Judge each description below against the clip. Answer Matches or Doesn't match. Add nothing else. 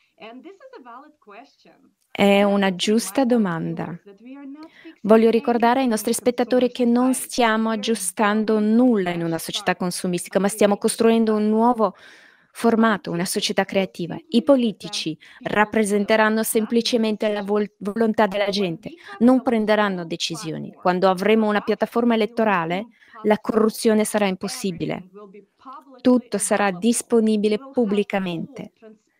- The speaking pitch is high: Matches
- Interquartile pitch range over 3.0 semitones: Doesn't match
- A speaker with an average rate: Doesn't match